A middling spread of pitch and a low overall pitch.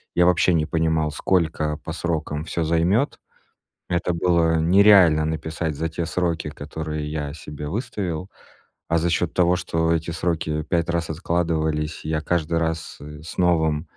No: narrow, 1.9 semitones; very low, 80 Hz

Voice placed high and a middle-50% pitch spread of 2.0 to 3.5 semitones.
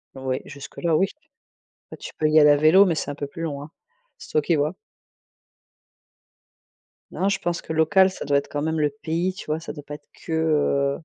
No: medium, 155 Hz; narrow, 2.5 semitones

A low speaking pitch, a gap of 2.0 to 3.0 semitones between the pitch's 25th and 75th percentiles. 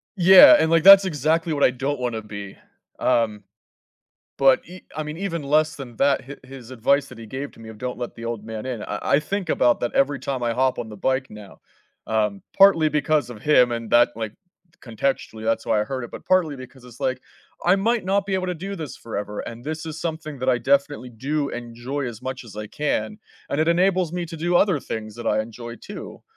No: low, 130 Hz; average, 5.3 semitones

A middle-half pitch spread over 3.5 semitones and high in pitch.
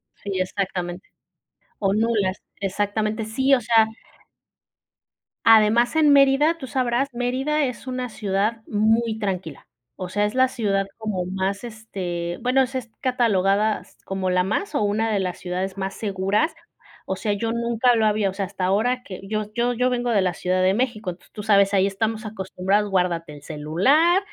Yes: average, 3.9 semitones; high, 215 Hz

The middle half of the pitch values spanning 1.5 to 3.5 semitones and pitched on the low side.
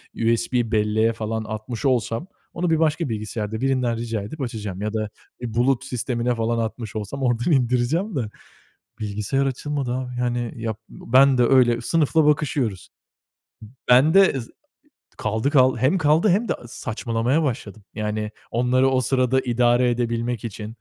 Yes: average, 3.1 semitones; low, 120 Hz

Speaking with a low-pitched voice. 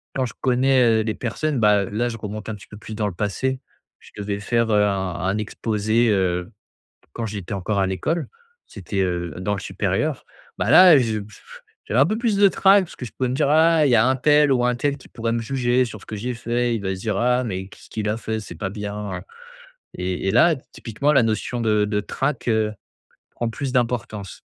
Yes: low, 110 Hz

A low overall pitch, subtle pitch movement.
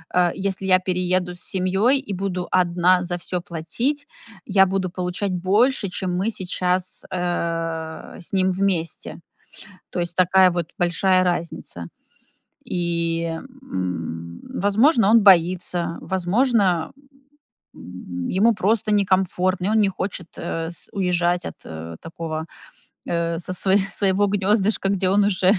No: medium, 185 Hz; narrow, 2.3 semitones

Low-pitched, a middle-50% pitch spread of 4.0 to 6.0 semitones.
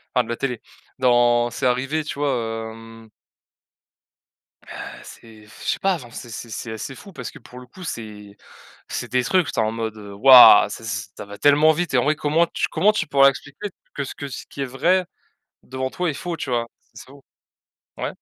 Yes: low, 125 Hz; average, 4.4 semitones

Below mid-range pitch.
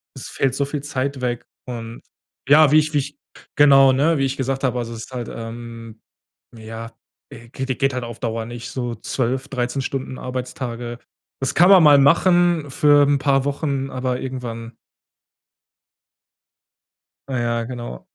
Yes: low, 130 Hz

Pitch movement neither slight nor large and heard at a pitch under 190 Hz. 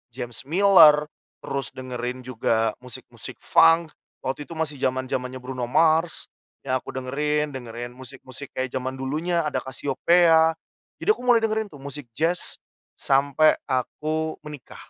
Yes: average, 3.7 semitones; medium, 140 Hz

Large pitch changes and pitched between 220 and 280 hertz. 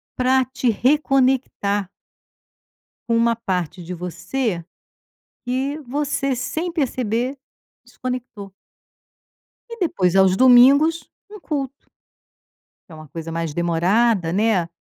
Yes: wide, 6.5 semitones; high, 240 Hz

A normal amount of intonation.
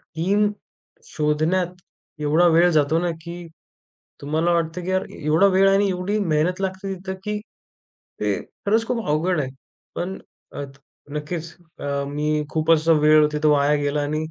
Yes: average, 3.7 semitones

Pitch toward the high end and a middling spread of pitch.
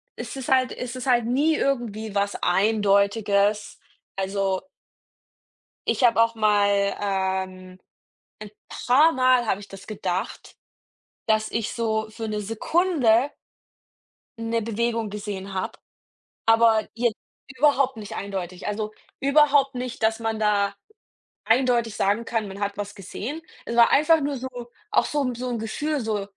Yes: high, 220 Hz; average, 3.6 semitones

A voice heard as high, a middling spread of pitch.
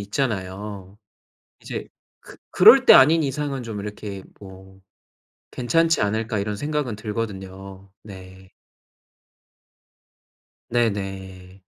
No: low, 105 Hz; average, 3.4 semitones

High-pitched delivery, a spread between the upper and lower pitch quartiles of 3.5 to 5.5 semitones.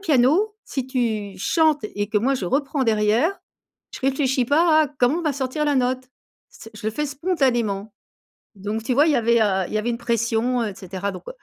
Yes: very high, 250 Hz; average, 5.0 semitones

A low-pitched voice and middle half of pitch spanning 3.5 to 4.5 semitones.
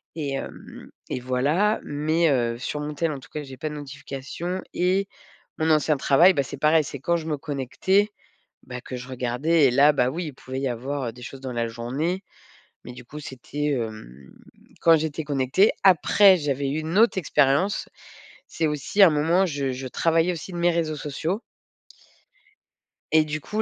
No: medium, 150 Hz; average, 4.0 semitones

